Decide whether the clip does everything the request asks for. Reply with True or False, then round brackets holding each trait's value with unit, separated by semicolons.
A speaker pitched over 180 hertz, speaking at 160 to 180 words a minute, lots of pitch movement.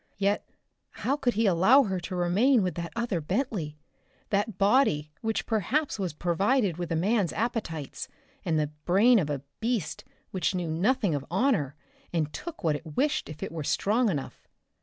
True (190 Hz; 175 wpm; 6.0 semitones)